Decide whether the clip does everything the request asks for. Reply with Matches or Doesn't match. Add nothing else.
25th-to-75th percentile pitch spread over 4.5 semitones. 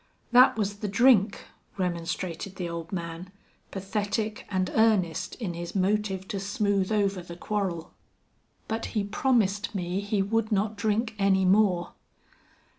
Doesn't match